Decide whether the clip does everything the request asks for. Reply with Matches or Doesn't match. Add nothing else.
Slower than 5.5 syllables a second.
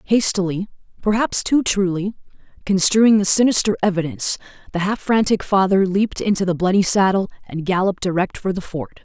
Doesn't match